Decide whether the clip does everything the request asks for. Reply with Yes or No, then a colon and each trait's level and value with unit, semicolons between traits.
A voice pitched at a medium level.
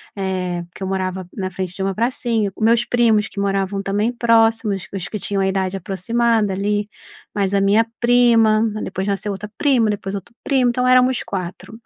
No: high, 205 Hz